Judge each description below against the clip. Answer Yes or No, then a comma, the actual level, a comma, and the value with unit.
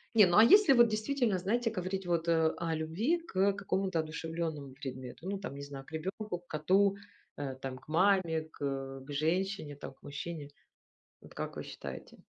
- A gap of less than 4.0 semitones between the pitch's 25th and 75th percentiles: No, average, 5.3 semitones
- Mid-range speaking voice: Yes, medium, 170 Hz